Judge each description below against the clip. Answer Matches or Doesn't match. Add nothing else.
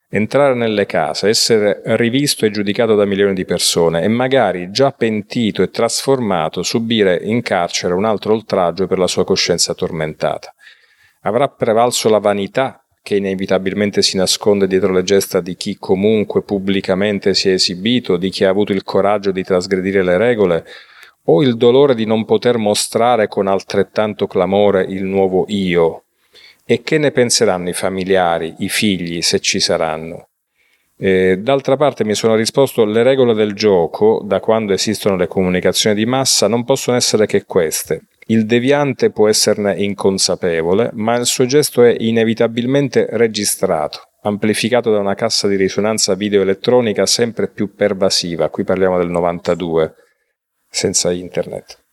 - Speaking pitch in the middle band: Doesn't match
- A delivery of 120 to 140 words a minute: Doesn't match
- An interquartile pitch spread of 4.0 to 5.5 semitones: Doesn't match